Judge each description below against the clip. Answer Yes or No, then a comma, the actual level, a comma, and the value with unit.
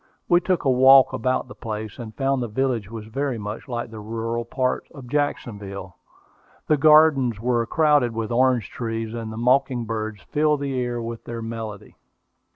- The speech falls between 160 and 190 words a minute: Yes, average, 175 wpm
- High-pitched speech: No, low, 120 Hz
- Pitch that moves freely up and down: No, average, 3.1 semitones